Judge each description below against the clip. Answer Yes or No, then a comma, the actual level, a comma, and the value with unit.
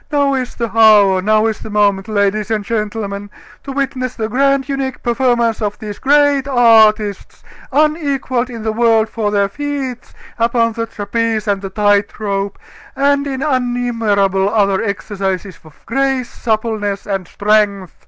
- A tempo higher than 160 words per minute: No, average, 150 wpm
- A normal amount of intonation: Yes, average, 3.8 semitones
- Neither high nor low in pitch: No, high, 220 Hz